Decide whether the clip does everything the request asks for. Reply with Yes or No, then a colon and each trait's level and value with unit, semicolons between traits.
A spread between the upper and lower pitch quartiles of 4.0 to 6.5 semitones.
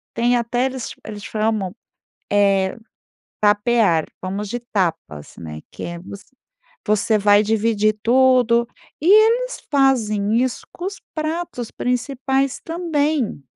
Yes: average, 4.6 semitones